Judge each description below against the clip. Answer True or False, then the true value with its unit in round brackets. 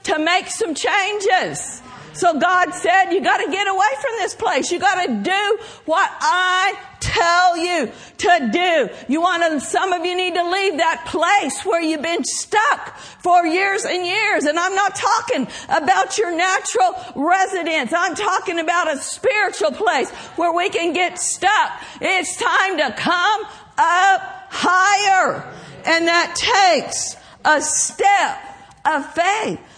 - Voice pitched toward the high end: True (365 Hz)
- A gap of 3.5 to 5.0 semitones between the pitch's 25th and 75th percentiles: False (2.6 semitones)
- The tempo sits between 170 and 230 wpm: False (145 wpm)